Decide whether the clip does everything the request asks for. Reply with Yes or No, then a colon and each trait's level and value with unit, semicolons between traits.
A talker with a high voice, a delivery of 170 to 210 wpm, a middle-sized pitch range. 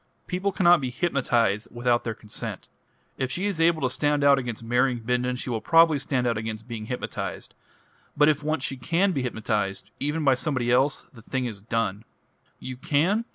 No: low, 130 Hz; average, 190 wpm; average, 4.5 semitones